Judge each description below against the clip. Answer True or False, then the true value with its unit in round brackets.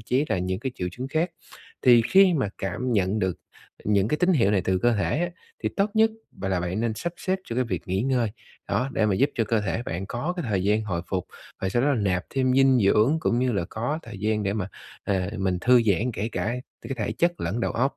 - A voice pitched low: True (115 Hz)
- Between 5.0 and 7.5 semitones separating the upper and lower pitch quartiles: True (5.3 semitones)